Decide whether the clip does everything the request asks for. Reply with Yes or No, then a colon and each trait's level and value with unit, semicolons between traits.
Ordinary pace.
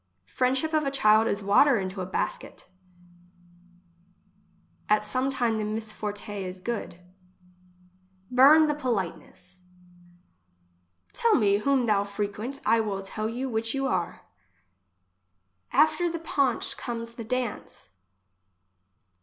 No: slow, 115 wpm